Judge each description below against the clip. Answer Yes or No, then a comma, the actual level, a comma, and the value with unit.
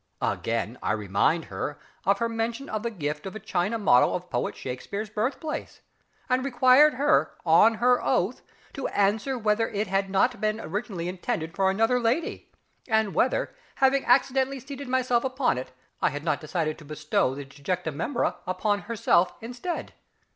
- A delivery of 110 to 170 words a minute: Yes, average, 165 wpm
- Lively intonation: Yes, wide, 6.2 semitones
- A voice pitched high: Yes, high, 215 Hz